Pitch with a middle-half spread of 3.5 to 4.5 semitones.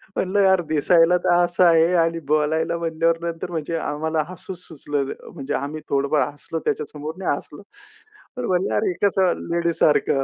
No: narrow, 2.6 semitones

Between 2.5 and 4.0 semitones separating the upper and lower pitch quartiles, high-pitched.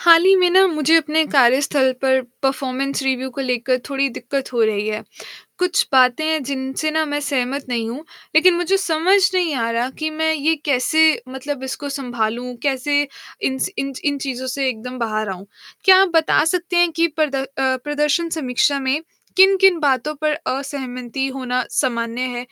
Yes: average, 3.7 semitones; very high, 275 Hz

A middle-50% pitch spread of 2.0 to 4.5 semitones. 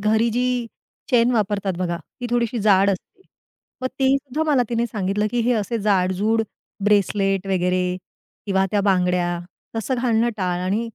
Yes: average, 3.7 semitones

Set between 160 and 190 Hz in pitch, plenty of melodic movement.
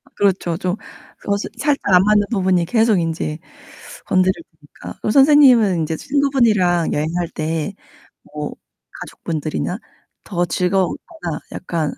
No: medium, 185 Hz; average, 4.4 semitones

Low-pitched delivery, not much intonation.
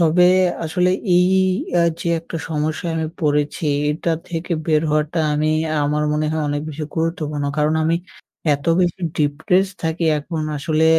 No: medium, 160 Hz; narrow, 1.9 semitones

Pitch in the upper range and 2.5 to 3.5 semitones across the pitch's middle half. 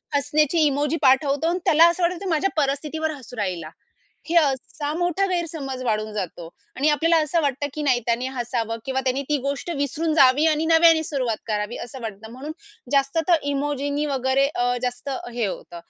No: very high, 280 Hz; average, 4.1 semitones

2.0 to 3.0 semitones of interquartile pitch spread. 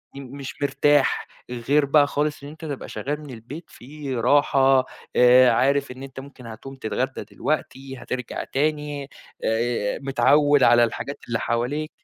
Yes: narrow, 2.6 semitones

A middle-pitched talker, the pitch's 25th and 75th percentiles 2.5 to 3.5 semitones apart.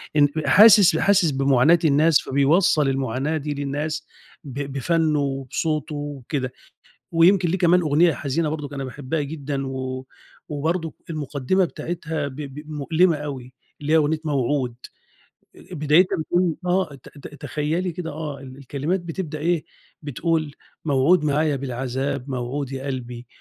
Yes: medium, 150 Hz; average, 3.1 semitones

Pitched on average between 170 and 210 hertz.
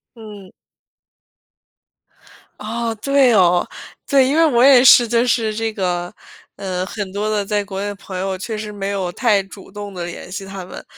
Yes: high, 205 Hz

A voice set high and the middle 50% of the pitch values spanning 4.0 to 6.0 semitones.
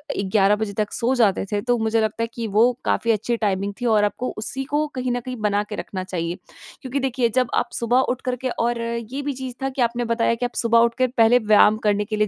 No: high, 230 Hz; average, 2.8 semitones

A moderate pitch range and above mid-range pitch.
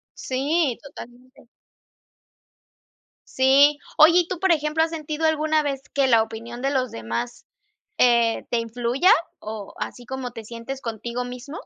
Yes: average, 4.3 semitones; very high, 260 Hz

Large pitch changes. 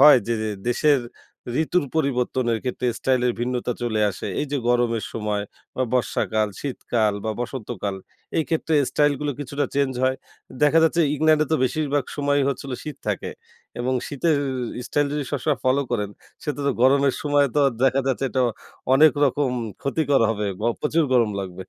No: average, 3.3 semitones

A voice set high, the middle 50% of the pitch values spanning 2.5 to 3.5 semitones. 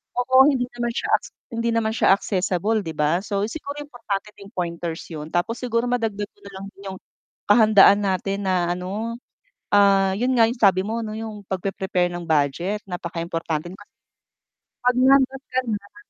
No: high, 200 Hz; average, 4.2 semitones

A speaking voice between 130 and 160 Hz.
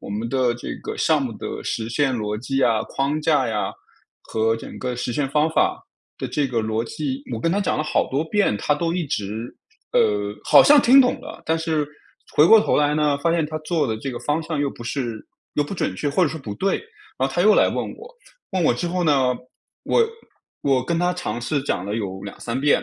Yes: medium, 140 Hz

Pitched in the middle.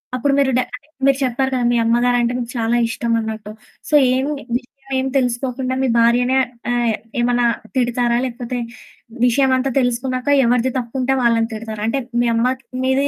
No: high, 245 Hz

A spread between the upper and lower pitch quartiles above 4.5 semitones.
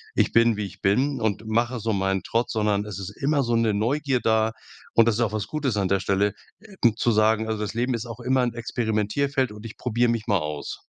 No: narrow, 2.6 semitones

